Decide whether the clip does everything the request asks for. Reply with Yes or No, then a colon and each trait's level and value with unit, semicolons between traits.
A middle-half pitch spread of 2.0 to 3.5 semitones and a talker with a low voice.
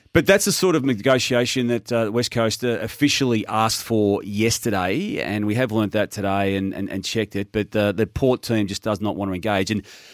Yes: average, 3.1 semitones; low, 110 Hz